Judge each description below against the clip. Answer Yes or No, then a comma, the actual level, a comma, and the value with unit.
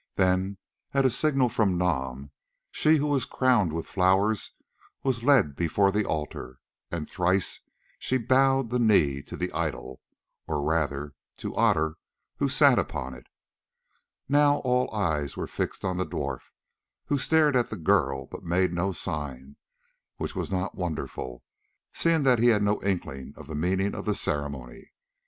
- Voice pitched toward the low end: Yes, very low, 95 Hz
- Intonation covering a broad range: Yes, wide, 8.2 semitones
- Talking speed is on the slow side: No, average, 160 wpm